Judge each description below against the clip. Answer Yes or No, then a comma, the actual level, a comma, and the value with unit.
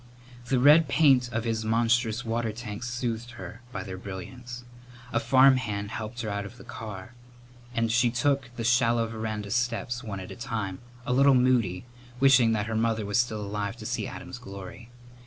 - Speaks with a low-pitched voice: Yes, low, 115 Hz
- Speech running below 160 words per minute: No, average, 180 wpm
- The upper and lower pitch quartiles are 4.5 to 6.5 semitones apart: No, narrow, 2.4 semitones